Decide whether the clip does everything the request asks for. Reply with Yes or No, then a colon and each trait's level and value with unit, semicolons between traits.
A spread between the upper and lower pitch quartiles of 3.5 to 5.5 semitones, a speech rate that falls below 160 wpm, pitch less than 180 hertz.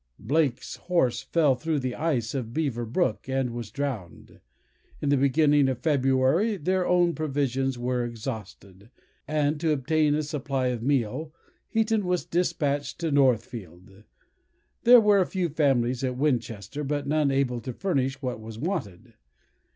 Yes: average, 4.2 semitones; average, 150 wpm; low, 135 Hz